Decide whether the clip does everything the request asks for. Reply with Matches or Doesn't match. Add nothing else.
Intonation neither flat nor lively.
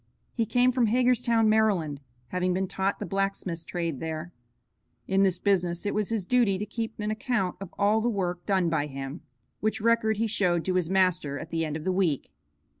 Matches